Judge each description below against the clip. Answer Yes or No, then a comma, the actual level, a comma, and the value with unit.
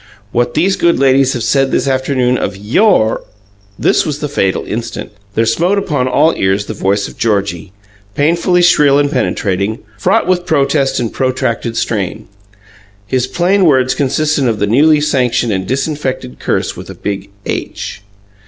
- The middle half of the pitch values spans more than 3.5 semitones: Yes, wide, 5.4 semitones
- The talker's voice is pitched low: Yes, low, 130 Hz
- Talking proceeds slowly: No, average, 160 wpm